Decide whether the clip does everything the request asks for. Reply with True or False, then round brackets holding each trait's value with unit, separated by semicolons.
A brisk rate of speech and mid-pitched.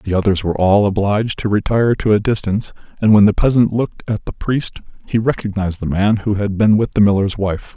False (225 wpm; 105 Hz)